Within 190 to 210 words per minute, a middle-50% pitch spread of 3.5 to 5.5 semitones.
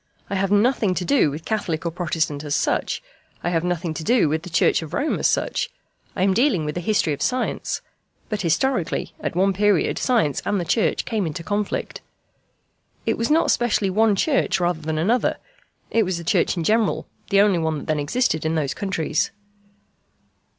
Yes: average, 195 wpm; average, 5.1 semitones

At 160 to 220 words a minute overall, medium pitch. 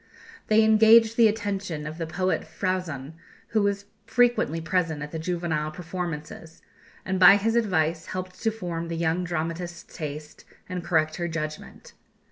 No: average, 150 wpm; medium, 175 Hz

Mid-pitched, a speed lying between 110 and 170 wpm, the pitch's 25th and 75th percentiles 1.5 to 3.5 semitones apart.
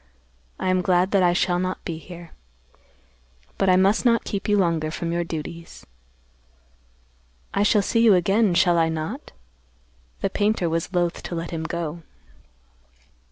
Yes: medium, 175 Hz; average, 160 wpm; narrow, 2.6 semitones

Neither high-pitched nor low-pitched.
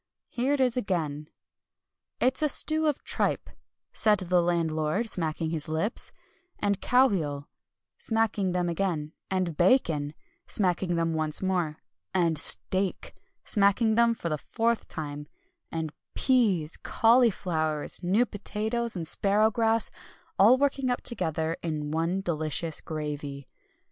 Yes: medium, 180 Hz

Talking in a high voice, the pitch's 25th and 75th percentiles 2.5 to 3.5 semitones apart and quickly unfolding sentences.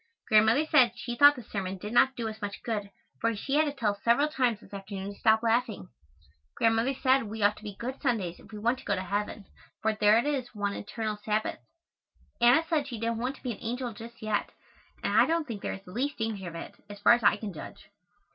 Yes: high, 225 Hz; average, 3.2 semitones; fast, 245 wpm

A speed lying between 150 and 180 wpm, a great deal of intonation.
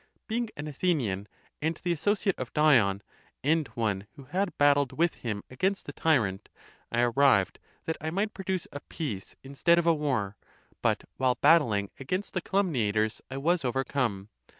Yes: average, 160 wpm; wide, 6.7 semitones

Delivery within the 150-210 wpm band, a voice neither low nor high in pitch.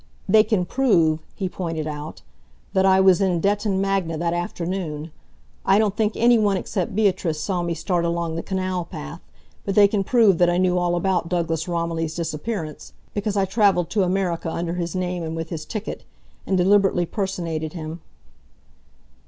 Yes: average, 175 wpm; medium, 180 Hz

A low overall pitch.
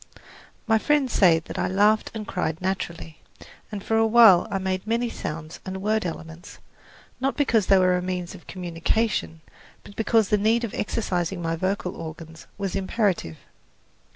No: high, 190 Hz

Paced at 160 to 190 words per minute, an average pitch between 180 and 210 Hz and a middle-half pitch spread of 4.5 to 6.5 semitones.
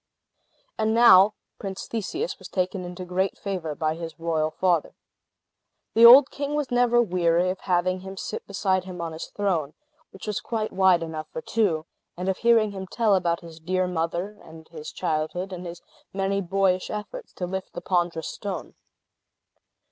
No: average, 170 wpm; medium, 185 Hz; average, 3.1 semitones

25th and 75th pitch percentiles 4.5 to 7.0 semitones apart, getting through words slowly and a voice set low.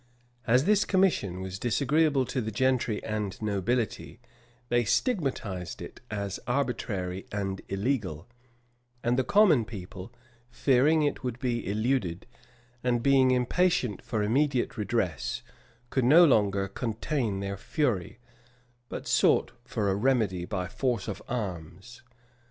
Yes: average, 5.0 semitones; slow, 130 wpm; low, 120 Hz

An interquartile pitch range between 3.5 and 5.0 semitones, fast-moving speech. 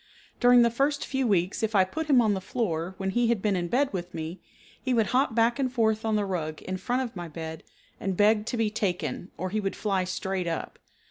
Yes: average, 4.4 semitones; fast, 245 wpm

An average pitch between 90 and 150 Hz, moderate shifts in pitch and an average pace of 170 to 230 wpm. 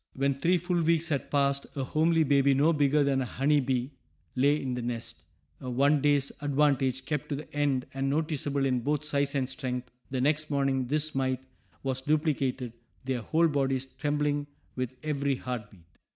No: medium, 140 Hz; narrow, 2.2 semitones; average, 180 wpm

